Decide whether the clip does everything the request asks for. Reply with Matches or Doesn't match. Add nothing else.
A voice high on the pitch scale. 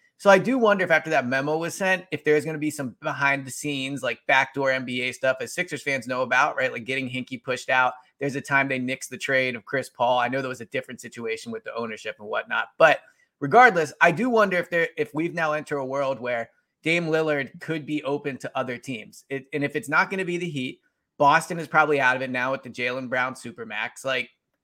Doesn't match